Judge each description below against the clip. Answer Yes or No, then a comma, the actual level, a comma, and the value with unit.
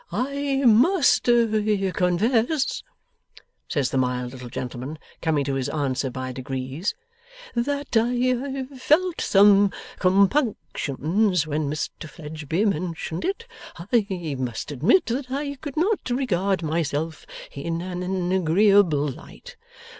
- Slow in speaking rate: Yes, slow, 110 wpm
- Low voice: No, medium, 185 Hz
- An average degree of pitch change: No, wide, 8.6 semitones